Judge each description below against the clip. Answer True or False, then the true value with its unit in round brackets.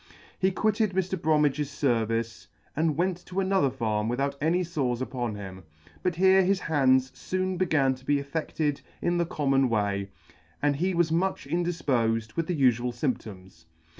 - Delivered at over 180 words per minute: False (160 wpm)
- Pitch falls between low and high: True (145 Hz)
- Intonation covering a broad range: True (6.2 semitones)